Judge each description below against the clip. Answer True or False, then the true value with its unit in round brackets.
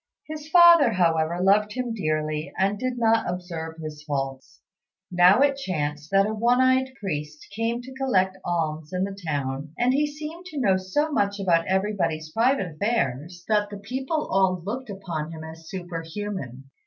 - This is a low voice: False (190 Hz)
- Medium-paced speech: True (165 wpm)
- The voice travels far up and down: True (7.0 semitones)